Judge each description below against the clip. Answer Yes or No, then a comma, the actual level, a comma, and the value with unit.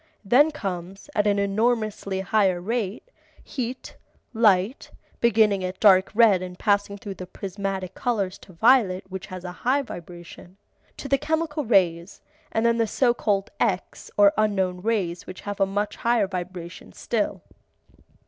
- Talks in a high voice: Yes, high, 200 Hz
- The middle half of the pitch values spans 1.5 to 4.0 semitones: Yes, average, 3.7 semitones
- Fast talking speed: No, average, 150 wpm